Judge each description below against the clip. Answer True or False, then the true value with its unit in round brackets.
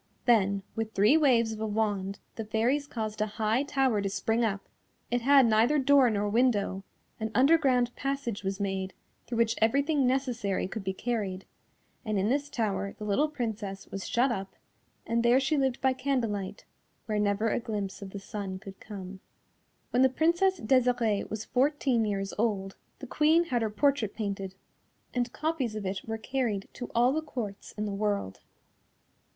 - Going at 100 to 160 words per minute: False (175 wpm)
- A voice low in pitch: False (225 Hz)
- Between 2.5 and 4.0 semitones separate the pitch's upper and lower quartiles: False (4.4 semitones)